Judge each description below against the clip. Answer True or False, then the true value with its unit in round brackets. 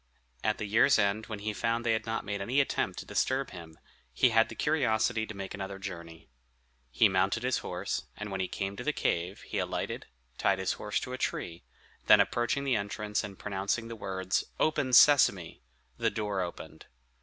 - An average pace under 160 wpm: False (195 wpm)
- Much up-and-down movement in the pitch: False (3.1 semitones)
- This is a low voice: True (105 Hz)